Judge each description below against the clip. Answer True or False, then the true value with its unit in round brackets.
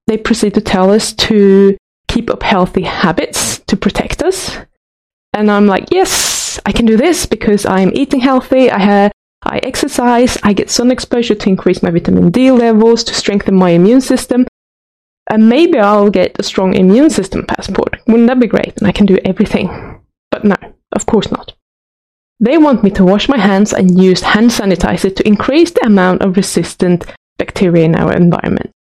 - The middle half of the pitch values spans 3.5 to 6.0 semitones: True (4.4 semitones)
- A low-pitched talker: False (210 Hz)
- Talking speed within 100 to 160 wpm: False (180 wpm)